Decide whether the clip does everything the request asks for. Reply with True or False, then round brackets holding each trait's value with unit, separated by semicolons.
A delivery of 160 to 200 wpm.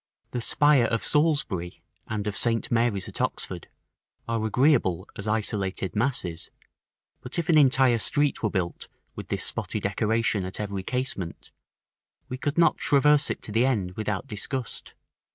False (150 wpm)